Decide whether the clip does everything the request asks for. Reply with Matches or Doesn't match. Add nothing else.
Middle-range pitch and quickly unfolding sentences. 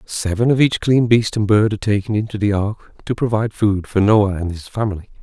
Doesn't match